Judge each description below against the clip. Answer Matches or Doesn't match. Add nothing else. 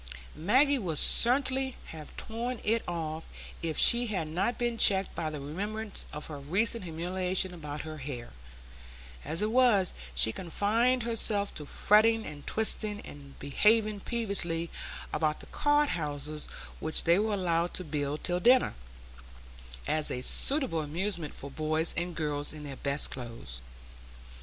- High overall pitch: Doesn't match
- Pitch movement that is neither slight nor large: Doesn't match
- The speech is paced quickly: Doesn't match